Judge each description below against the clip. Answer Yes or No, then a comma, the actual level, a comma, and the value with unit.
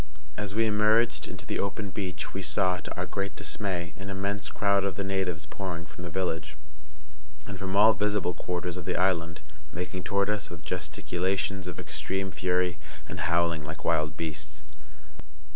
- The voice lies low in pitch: Yes, very low, 95 Hz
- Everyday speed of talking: Yes, average, 170 wpm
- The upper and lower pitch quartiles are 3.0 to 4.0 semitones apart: No, narrow, 2.5 semitones